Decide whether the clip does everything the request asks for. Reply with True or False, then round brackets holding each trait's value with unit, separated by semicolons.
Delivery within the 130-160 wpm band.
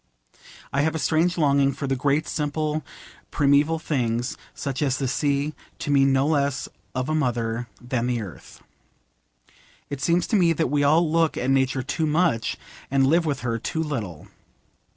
False (170 wpm)